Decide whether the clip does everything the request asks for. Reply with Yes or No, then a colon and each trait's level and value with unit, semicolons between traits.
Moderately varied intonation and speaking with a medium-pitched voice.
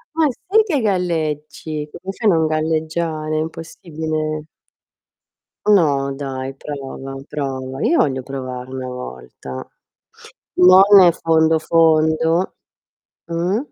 Yes: average, 3.6 semitones; medium, 155 Hz